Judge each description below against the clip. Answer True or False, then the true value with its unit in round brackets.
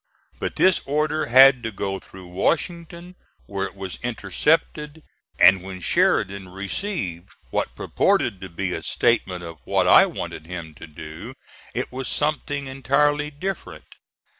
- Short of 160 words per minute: True (140 wpm)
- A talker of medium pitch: False (115 Hz)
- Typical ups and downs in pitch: False (8.0 semitones)